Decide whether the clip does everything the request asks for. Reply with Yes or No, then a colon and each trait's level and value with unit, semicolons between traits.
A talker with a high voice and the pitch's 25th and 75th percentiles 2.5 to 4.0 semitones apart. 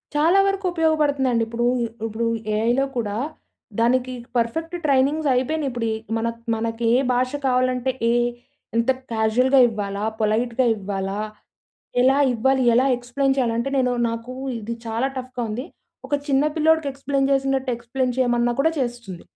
Yes: very high, 250 Hz; average, 2.8 semitones